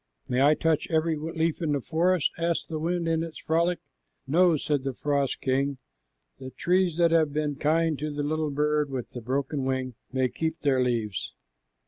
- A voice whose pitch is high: No, medium, 150 Hz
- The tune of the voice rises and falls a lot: No, average, 3.2 semitones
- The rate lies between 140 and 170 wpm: No, average, 185 wpm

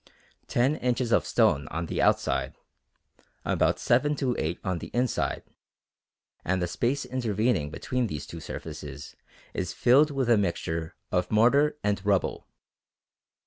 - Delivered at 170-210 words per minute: No, average, 140 wpm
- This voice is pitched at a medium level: No, low, 110 Hz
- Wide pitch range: Yes, wide, 6.6 semitones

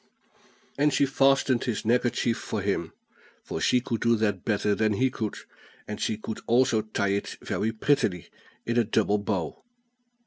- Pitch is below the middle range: Yes, low, 110 Hz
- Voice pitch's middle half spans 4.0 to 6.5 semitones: No, average, 2.9 semitones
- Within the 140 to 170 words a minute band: Yes, average, 165 wpm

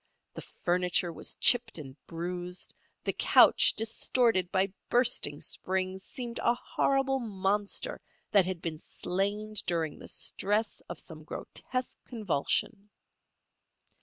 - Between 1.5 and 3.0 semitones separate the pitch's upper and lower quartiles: No, average, 4.5 semitones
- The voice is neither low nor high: No, high, 195 Hz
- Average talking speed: No, slow, 115 wpm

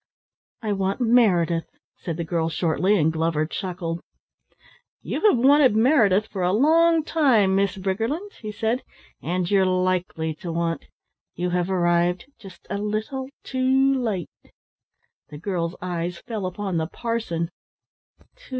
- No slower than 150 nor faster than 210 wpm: No, slow, 135 wpm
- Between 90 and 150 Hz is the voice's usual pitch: No, high, 190 Hz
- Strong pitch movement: No, average, 4.9 semitones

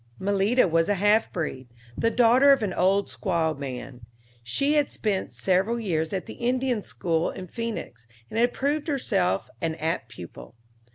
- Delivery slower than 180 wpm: Yes, average, 165 wpm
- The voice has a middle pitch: No, high, 195 Hz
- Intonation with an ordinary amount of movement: No, wide, 6.7 semitones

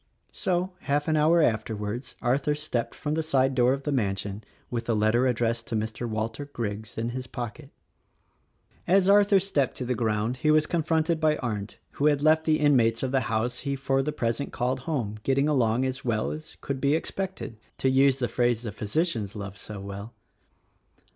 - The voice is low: Yes, low, 130 Hz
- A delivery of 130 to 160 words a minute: No, average, 195 wpm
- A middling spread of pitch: Yes, average, 4.9 semitones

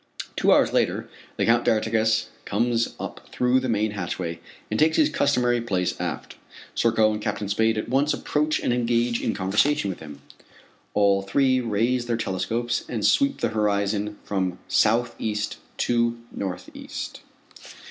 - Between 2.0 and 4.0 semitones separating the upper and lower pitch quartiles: Yes, average, 3.0 semitones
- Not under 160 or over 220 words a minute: No, average, 145 wpm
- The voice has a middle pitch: No, low, 110 Hz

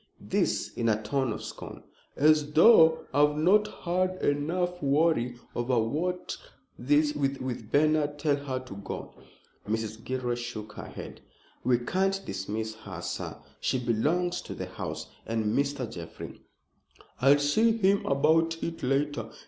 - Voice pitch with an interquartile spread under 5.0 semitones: No, average, 5.3 semitones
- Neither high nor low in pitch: Yes, medium, 145 Hz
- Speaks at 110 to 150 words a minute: Yes, average, 140 wpm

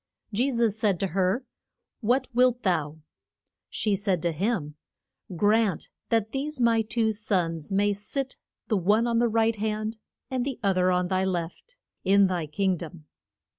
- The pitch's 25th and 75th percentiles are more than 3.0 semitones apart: Yes, average, 4.0 semitones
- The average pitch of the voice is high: Yes, high, 205 Hz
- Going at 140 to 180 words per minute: Yes, average, 165 wpm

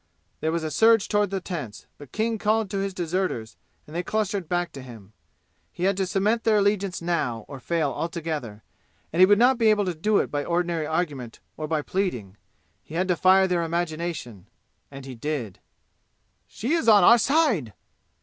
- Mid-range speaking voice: Yes, medium, 175 Hz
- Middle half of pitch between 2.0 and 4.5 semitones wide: No, average, 5.2 semitones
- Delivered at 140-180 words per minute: No, average, 190 wpm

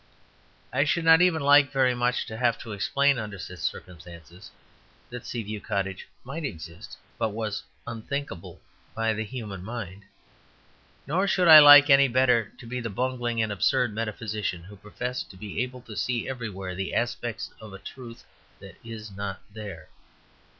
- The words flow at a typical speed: Yes, average, 165 wpm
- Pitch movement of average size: Yes, average, 4.2 semitones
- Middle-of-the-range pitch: No, low, 115 Hz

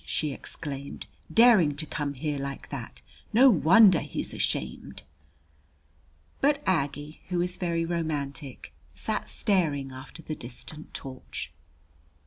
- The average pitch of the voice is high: No, medium, 150 Hz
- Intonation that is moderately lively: Yes, average, 4.3 semitones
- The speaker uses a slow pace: Yes, slow, 115 wpm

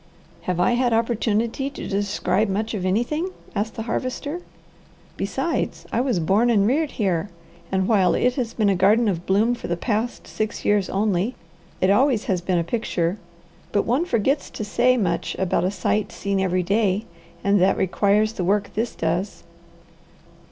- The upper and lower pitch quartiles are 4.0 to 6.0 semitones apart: No, average, 3.6 semitones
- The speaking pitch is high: Yes, high, 210 Hz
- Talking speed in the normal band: Yes, average, 175 wpm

